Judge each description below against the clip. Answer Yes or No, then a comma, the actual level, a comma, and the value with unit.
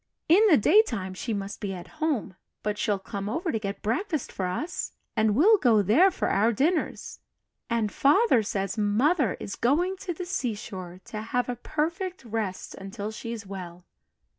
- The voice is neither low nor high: No, high, 225 Hz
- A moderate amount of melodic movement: No, wide, 7.7 semitones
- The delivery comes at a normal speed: Yes, average, 170 wpm